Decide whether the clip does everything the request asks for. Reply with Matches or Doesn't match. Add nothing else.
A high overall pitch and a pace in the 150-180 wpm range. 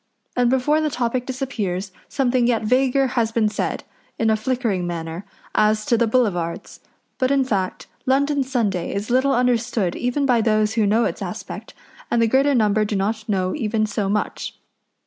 Matches